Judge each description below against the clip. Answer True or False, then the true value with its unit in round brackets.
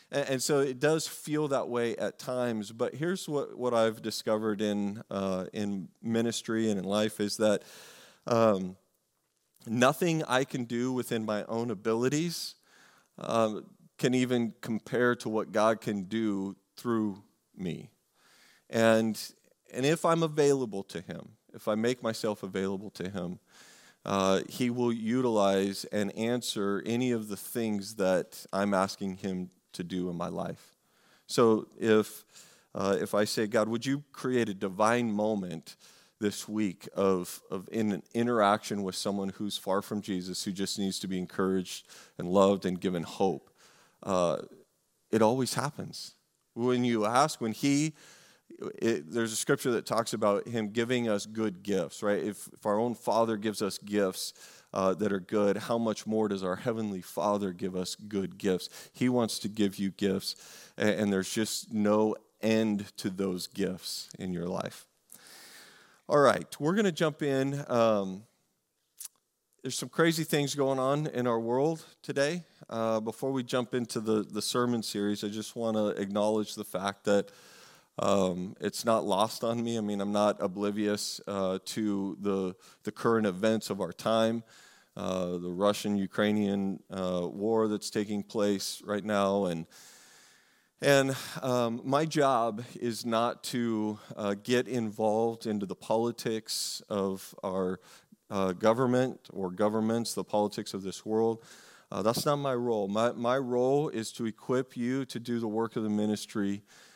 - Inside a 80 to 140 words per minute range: False (165 wpm)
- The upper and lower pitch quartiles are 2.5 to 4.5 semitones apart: True (3.4 semitones)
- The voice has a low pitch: True (110 Hz)